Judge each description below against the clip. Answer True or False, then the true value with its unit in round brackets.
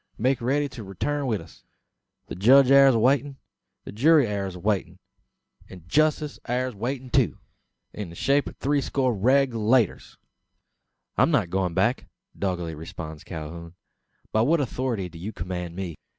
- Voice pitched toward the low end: True (115 Hz)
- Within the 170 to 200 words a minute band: False (150 wpm)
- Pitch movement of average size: False (6.8 semitones)